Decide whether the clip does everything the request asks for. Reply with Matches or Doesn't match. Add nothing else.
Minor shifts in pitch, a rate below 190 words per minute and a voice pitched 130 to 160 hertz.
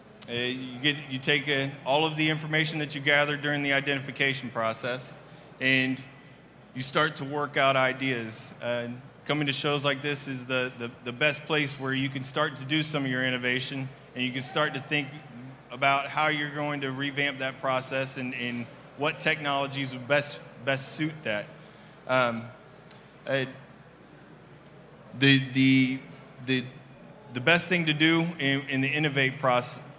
Matches